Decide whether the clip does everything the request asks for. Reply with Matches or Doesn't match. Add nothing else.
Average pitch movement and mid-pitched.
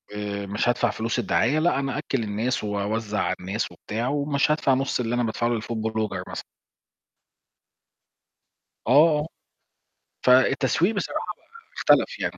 Doesn't match